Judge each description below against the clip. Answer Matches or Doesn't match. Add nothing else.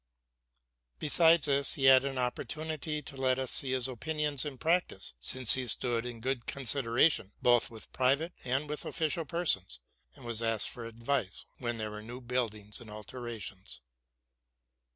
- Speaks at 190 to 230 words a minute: Doesn't match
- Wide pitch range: Doesn't match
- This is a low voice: Matches